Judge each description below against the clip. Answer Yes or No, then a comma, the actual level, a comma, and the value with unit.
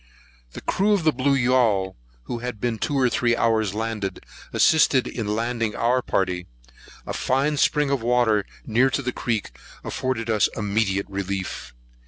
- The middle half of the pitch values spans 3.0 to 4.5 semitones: Yes, average, 3.7 semitones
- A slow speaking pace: No, average, 160 wpm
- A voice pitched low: Yes, low, 115 Hz